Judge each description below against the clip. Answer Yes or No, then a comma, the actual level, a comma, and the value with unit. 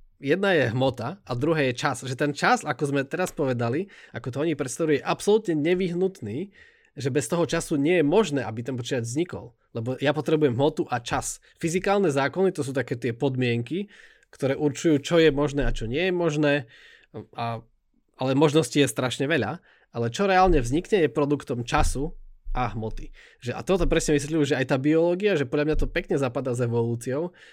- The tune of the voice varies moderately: Yes, average, 4.2 semitones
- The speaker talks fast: Yes, fast, 190 wpm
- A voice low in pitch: No, medium, 145 Hz